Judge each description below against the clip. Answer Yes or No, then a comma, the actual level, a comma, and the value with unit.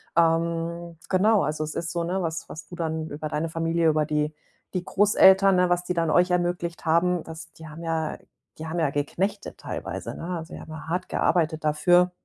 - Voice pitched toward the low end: No, medium, 165 Hz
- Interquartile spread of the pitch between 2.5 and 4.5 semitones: No, narrow, 2.0 semitones